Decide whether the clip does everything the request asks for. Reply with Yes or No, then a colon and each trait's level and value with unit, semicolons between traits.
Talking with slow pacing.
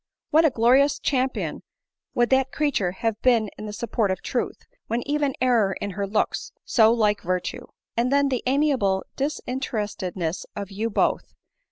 No: average, 160 wpm